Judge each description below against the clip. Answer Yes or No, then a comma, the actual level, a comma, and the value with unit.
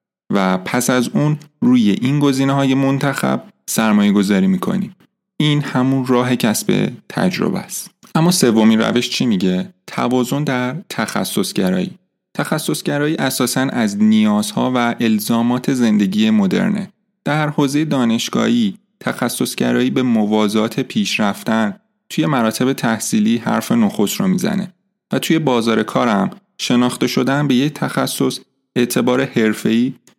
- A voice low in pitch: No, medium, 150 Hz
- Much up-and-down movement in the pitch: Yes, wide, 8.3 semitones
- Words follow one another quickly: No, average, 120 wpm